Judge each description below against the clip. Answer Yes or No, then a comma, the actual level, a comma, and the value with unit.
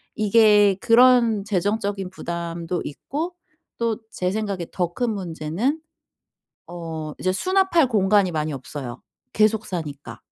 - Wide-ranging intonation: No, average, 4.8 semitones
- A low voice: No, high, 195 Hz